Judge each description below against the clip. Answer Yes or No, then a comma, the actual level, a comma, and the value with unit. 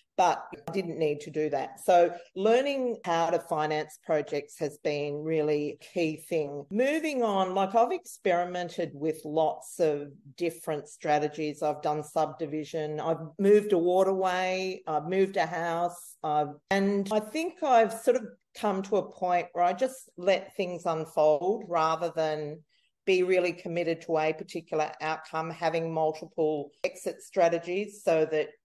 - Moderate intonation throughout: Yes, average, 3.9 semitones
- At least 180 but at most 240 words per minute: No, average, 150 wpm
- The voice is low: No, medium, 170 Hz